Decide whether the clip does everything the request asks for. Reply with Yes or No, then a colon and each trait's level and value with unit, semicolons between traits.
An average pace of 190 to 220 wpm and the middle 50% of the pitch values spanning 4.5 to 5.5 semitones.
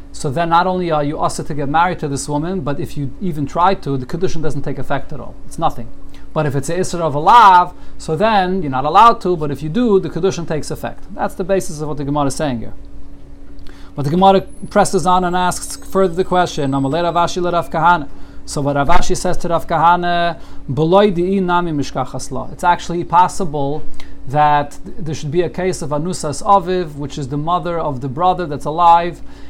No: average, 195 wpm; average, 3.8 semitones